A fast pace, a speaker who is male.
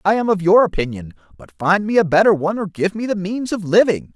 Yes: fast, 260 wpm; male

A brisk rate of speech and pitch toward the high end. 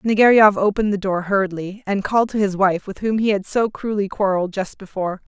Yes: fast, 215 wpm; high, 200 Hz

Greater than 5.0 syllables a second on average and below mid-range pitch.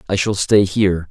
Yes: 5.4 syllables/s; low, 100 Hz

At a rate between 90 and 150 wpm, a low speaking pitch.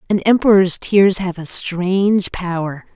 No: average, 140 wpm; medium, 185 Hz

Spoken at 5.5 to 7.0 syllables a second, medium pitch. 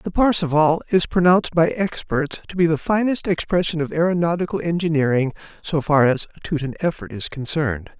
Yes: 5.6 syllables/s; medium, 160 Hz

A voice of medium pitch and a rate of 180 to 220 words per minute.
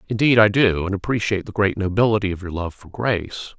No: low, 100 Hz; average, 200 wpm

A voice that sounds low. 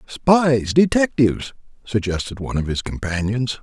Yes: low, 125 Hz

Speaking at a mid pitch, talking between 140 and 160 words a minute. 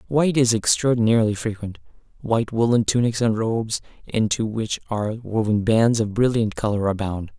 No: low, 110 Hz; average, 145 wpm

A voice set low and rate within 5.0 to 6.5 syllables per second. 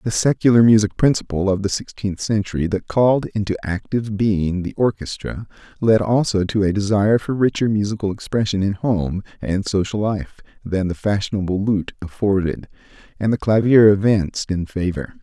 Yes: low, 100 Hz; 5.2 syllables/s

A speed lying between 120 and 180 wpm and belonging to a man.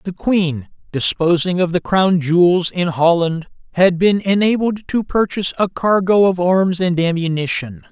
Yes: average, 150 wpm; male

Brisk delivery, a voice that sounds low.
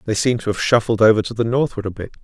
Yes: fast, 295 wpm; low, 110 Hz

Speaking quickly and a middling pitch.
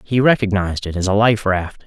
No: fast, 225 wpm; low, 100 Hz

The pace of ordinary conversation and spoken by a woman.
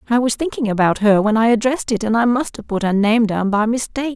No: fast, 275 wpm; female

